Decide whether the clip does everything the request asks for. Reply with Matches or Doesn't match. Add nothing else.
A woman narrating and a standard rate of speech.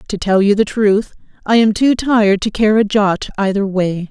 Doesn't match